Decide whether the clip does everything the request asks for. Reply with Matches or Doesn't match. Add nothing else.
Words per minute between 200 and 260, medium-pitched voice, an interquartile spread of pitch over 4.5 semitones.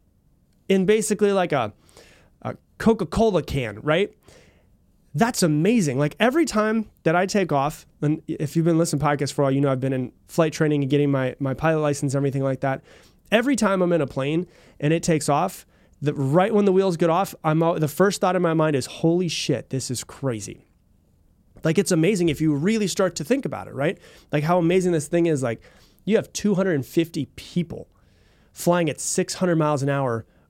Matches